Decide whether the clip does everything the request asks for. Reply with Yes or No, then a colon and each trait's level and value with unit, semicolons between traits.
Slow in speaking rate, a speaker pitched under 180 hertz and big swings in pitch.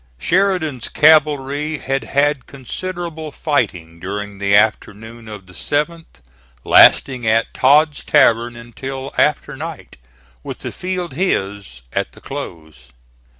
Yes: slow, 115 wpm; low, 135 Hz; wide, 6.5 semitones